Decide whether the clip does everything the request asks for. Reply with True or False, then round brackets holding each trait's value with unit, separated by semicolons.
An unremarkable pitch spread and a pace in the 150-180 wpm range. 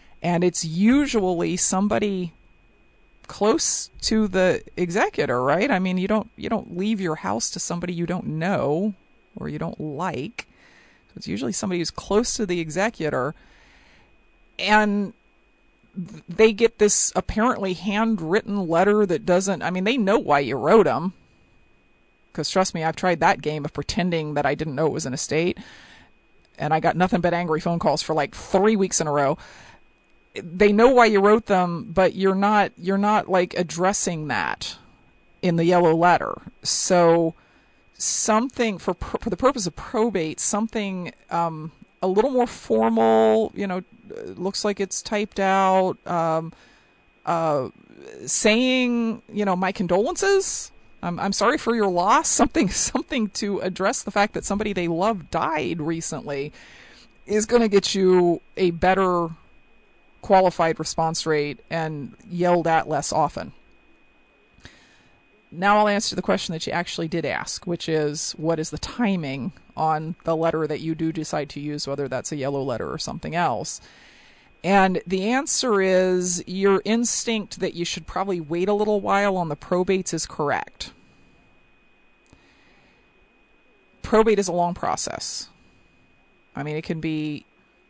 True (4.1 semitones; 155 wpm)